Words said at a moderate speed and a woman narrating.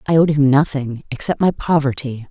Yes: average, 180 wpm; female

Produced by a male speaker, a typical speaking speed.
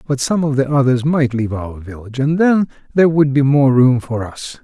No: male; fast, 235 wpm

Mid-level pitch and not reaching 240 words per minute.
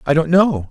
No: medium, 160 Hz; fast, 255 wpm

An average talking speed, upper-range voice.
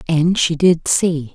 No: average, 180 wpm; medium, 165 Hz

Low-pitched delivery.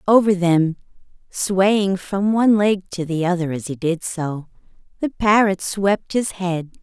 No: medium, 185 Hz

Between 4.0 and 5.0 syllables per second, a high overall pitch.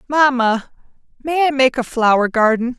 Yes: 4.7 syllables/s; very high, 255 Hz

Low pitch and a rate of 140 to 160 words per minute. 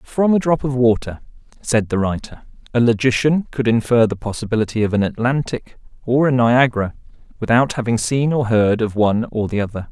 No: low, 120 Hz; average, 180 wpm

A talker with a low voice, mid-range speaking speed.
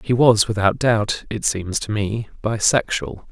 Yes: low, 110 Hz; average, 165 wpm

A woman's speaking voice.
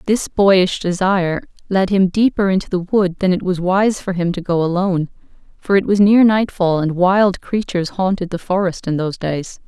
Yes: female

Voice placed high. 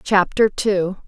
Yes: high, 195 Hz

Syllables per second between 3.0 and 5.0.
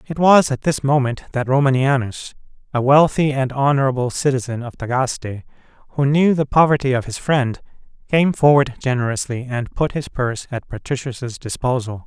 No: 5.3 syllables/s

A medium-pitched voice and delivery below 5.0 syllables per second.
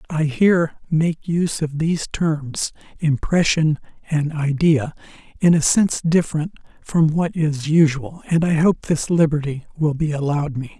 Yes: medium, 155 Hz; 4.5 syllables/s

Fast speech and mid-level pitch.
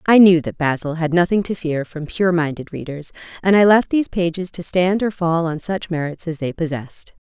Yes: fast, 225 wpm; medium, 170 Hz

